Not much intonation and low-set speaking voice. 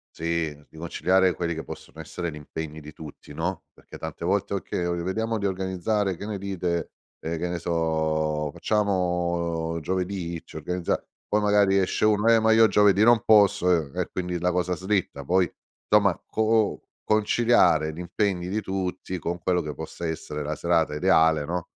No: average, 3.3 semitones; very low, 90 Hz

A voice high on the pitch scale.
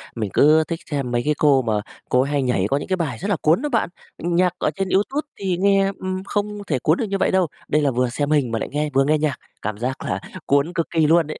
No: medium, 155 Hz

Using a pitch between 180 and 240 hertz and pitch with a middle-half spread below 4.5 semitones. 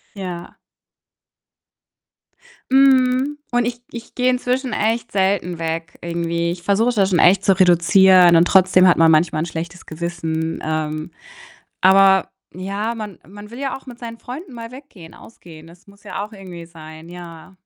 No: high, 190 Hz; average, 5.2 semitones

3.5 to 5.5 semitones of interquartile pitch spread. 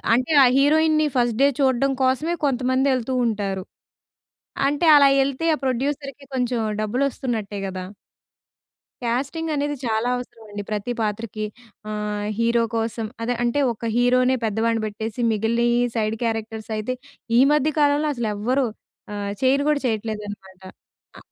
Yes: average, 3.8 semitones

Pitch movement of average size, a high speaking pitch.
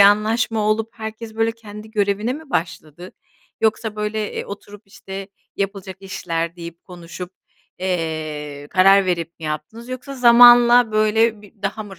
Yes: average, 3.6 semitones; high, 205 Hz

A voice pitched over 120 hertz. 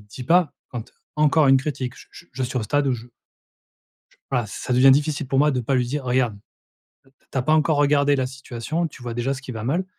Yes: low, 135 Hz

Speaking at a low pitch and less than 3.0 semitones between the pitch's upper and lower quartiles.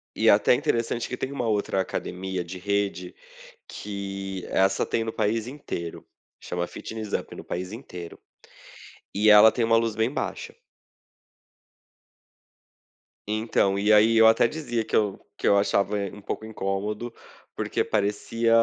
Yes: low, 105 Hz; narrow, 2.6 semitones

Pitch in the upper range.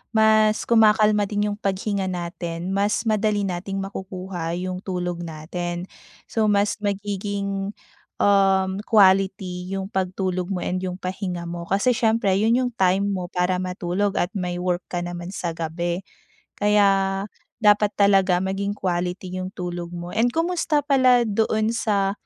Yes: high, 195 Hz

